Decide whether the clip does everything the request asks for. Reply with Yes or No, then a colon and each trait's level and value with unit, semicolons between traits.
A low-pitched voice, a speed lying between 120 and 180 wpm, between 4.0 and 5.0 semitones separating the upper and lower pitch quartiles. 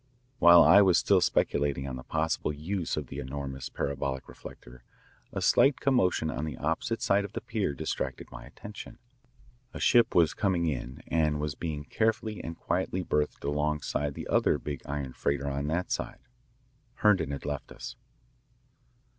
Yes: very low, 75 Hz; average, 165 wpm; average, 4.4 semitones